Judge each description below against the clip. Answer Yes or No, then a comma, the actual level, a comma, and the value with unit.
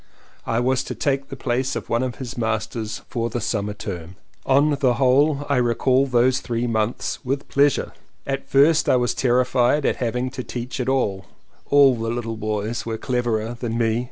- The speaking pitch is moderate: No, low, 125 Hz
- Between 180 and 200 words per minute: Yes, average, 185 wpm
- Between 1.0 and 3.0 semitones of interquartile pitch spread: Yes, average, 2.7 semitones